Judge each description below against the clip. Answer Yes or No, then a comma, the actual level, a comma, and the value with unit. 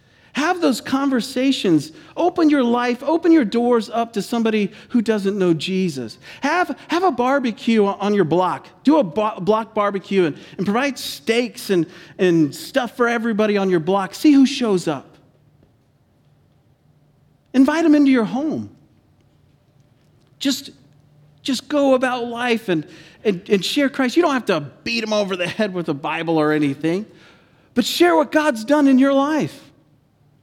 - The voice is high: Yes, high, 215 Hz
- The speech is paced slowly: No, average, 160 wpm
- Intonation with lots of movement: Yes, wide, 8.4 semitones